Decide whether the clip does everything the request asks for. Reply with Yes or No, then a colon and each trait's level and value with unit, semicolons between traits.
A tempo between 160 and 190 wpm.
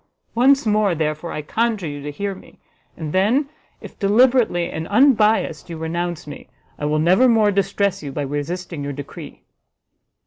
Yes: average, 165 wpm